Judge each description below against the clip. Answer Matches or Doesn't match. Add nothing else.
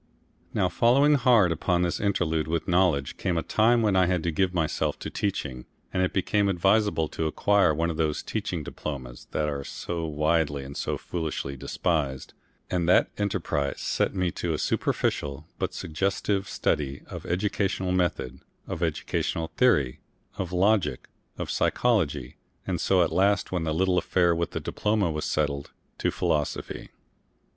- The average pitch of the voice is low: Matches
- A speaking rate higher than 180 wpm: Doesn't match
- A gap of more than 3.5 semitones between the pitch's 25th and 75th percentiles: Matches